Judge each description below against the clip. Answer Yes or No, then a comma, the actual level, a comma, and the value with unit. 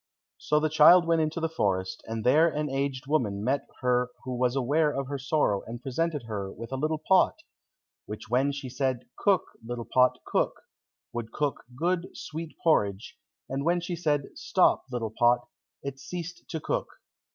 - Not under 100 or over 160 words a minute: No, average, 175 wpm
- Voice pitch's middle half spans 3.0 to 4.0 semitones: No, average, 4.5 semitones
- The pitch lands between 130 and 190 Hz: Yes, low, 135 Hz